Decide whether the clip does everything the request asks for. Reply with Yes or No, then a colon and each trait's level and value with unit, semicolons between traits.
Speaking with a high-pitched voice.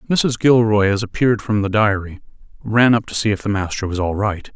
No: low, 105 Hz